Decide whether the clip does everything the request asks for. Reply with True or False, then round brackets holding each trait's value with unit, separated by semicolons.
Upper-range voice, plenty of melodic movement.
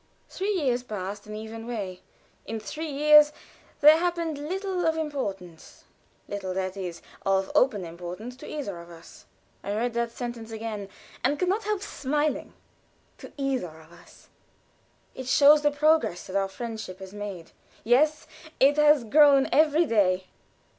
True (240 Hz; 7.5 semitones)